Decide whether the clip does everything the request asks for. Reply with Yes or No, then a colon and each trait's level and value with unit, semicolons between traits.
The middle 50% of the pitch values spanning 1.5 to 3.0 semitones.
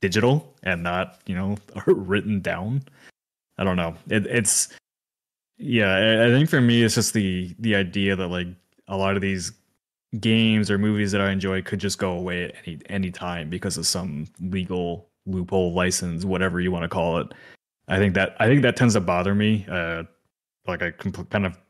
Yes: average, 2.7 semitones